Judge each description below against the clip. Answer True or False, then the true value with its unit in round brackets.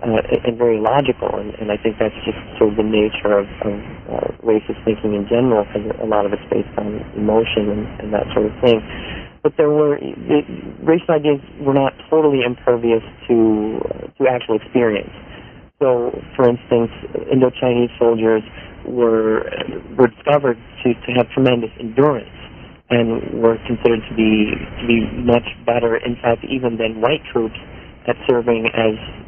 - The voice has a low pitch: True (115 Hz)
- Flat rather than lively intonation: True (2.0 semitones)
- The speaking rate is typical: True (170 wpm)